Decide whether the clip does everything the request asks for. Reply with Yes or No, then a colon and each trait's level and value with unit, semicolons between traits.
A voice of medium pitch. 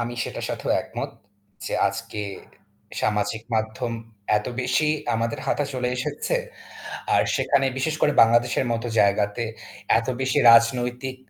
No: low, 120 Hz